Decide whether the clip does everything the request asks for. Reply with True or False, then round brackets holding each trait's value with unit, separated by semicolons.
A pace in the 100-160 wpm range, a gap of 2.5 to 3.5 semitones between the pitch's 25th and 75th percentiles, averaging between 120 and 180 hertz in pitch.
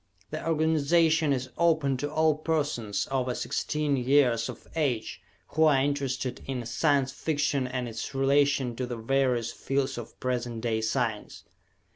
True (145 wpm; 3.1 semitones; 135 Hz)